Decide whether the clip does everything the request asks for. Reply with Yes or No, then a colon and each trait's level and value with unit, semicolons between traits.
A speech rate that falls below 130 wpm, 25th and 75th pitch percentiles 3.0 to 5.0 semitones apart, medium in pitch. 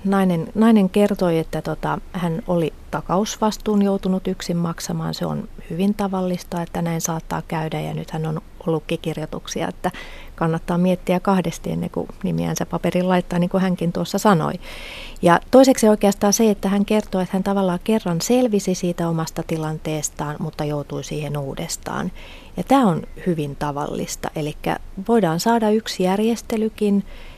No: average, 150 wpm; average, 3.8 semitones; medium, 180 Hz